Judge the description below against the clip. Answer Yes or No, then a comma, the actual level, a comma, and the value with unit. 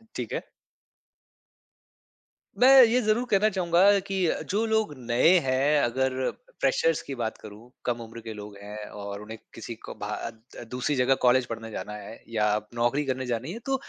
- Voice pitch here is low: Yes, low, 125 Hz